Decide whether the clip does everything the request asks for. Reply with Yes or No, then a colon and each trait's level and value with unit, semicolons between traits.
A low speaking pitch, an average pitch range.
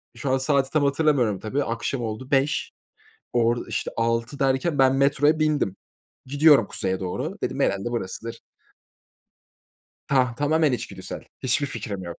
Yes: low, 130 Hz; average, 3.7 semitones